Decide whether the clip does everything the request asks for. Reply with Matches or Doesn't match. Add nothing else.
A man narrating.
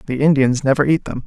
Matches